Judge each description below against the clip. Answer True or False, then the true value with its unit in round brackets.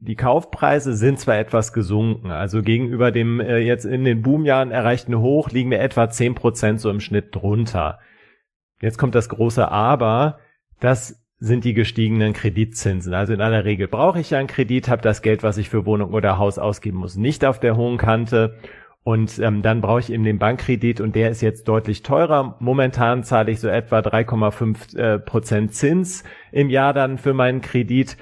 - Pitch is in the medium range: False (115 Hz)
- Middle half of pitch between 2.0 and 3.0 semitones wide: True (2.7 semitones)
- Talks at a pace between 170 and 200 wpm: True (185 wpm)